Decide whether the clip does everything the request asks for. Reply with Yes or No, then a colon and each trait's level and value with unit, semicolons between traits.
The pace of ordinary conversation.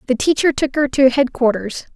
Yes: average, 185 wpm